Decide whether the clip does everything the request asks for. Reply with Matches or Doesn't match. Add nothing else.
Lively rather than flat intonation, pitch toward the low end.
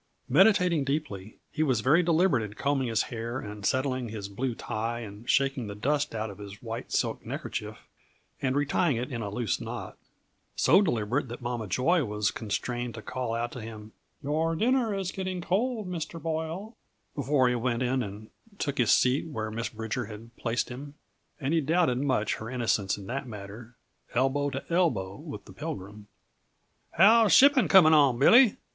Matches